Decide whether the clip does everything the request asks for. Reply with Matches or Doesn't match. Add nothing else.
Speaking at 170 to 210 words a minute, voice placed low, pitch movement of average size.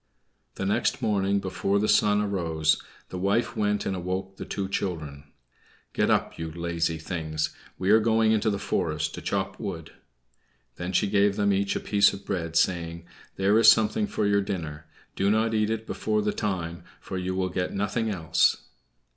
Matches